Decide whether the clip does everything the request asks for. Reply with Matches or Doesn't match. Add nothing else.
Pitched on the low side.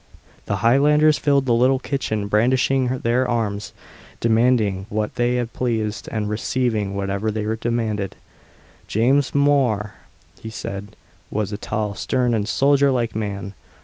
Matches